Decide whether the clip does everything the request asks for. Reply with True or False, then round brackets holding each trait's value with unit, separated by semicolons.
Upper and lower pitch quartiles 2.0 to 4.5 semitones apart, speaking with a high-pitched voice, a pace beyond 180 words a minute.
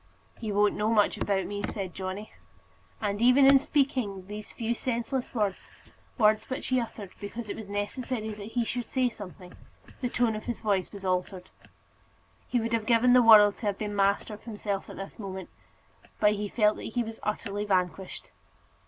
True (2.7 semitones; 210 Hz; 190 wpm)